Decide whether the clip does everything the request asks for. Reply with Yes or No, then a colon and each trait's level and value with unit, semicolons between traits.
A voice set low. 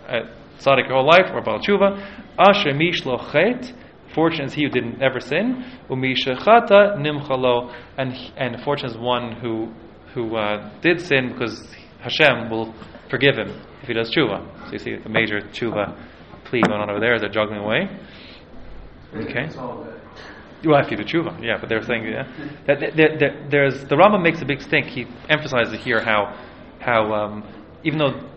Yes: low, 125 Hz